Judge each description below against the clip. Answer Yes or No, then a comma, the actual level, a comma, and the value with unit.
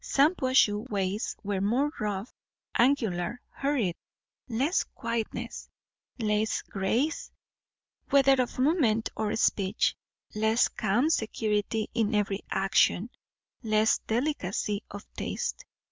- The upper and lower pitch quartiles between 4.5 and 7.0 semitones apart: No, average, 3.9 semitones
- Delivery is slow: Yes, slow, 100 wpm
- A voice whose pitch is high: Yes, high, 220 Hz